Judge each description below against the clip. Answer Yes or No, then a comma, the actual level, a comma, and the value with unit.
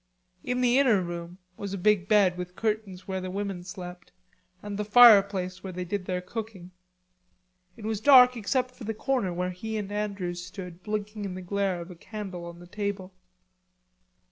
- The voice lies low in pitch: No, high, 195 Hz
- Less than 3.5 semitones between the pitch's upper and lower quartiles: Yes, average, 2.8 semitones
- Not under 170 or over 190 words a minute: Yes, average, 185 wpm